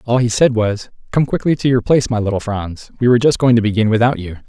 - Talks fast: Yes, fast, 270 wpm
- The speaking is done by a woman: No, male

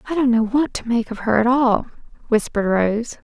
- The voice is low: No, high, 235 Hz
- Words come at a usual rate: No, fast, 220 wpm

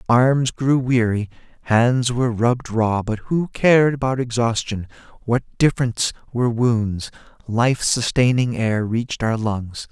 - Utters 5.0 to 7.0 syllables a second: No, 4.3 syllables/s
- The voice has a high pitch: No, low, 120 Hz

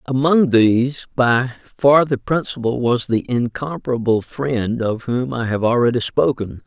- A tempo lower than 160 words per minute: Yes, average, 145 wpm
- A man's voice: Yes, male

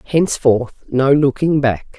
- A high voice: No, low, 135 Hz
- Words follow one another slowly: Yes, slow, 120 wpm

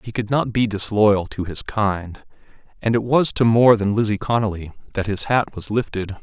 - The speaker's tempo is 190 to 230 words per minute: Yes, average, 200 wpm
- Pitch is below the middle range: Yes, low, 110 Hz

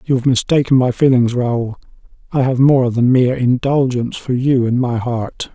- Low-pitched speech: Yes, low, 125 Hz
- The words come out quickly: No, average, 185 wpm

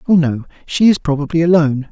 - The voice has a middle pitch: Yes, medium, 155 Hz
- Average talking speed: Yes, average, 190 wpm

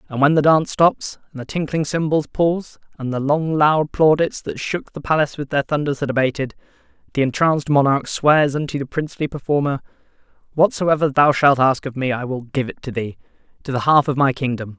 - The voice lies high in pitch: No, medium, 145 Hz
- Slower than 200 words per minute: No, fast, 205 wpm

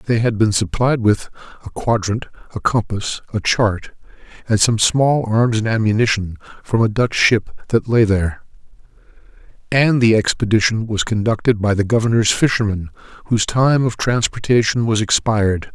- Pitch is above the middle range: No, low, 110 Hz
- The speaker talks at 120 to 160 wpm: Yes, average, 150 wpm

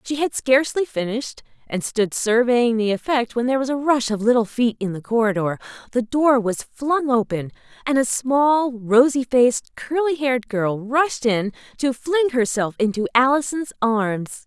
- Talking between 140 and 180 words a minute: Yes, average, 170 wpm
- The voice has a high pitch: Yes, high, 245 Hz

